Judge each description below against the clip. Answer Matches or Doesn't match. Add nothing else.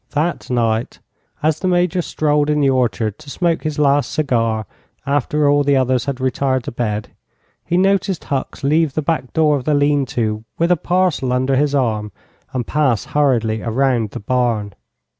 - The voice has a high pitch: Doesn't match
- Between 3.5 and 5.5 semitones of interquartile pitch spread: Matches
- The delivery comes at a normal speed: Matches